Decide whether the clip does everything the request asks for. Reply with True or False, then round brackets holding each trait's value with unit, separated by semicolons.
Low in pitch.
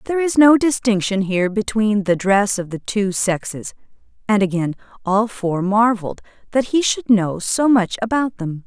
False (210 Hz)